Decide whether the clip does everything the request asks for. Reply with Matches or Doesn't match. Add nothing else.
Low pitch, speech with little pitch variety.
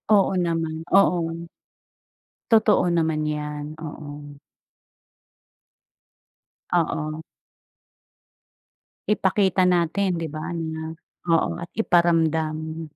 Doesn't match